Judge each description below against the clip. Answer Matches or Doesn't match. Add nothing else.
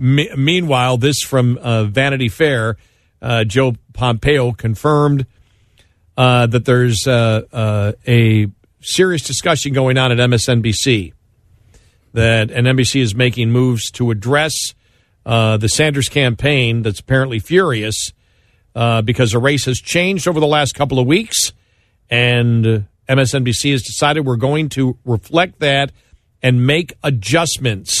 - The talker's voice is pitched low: Matches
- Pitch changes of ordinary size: Matches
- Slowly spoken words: Matches